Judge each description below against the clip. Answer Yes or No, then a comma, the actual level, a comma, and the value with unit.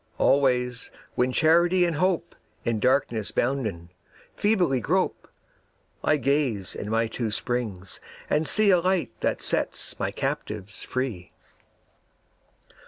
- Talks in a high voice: No, low, 130 Hz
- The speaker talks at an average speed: No, slow, 115 wpm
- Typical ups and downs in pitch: No, wide, 6.6 semitones